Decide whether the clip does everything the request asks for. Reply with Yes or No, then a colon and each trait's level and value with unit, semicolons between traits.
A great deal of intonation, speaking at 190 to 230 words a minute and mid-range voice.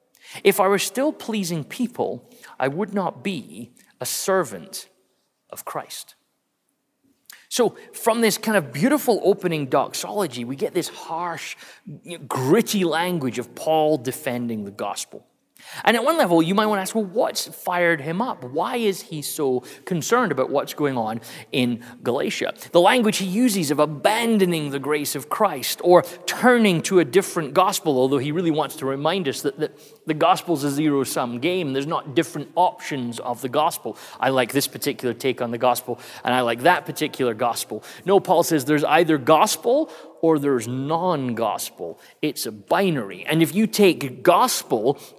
No: wide, 5.8 semitones; average, 170 wpm; medium, 160 Hz